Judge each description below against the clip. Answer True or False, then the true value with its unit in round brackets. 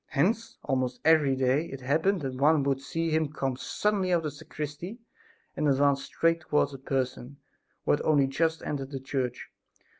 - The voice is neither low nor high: True (145 Hz)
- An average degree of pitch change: True (3.1 semitones)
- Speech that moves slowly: False (180 wpm)